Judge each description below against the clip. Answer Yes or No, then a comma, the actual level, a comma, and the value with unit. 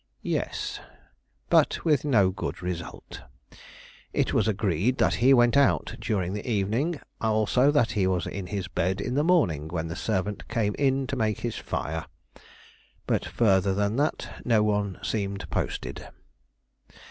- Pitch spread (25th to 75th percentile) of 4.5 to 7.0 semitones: Yes, average, 4.8 semitones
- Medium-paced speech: Yes, average, 145 wpm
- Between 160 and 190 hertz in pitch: No, low, 105 Hz